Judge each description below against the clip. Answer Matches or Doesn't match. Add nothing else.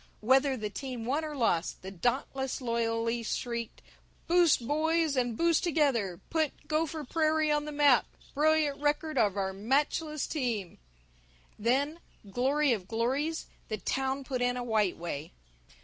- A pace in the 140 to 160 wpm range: Matches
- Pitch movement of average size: Matches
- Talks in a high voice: Matches